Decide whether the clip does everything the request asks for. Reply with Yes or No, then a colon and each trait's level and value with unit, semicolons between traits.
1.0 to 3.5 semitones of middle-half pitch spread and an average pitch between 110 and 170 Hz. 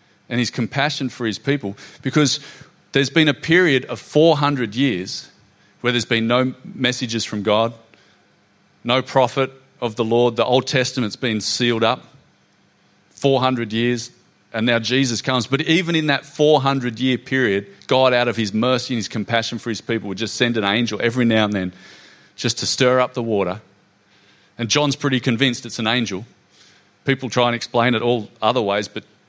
Yes: average, 2.8 semitones; low, 120 Hz